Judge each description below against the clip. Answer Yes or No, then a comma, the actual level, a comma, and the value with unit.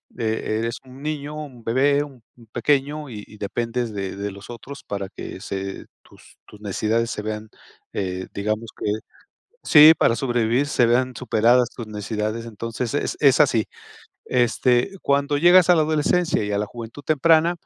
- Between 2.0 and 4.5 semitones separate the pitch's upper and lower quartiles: No, average, 4.9 semitones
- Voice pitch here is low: Yes, low, 120 Hz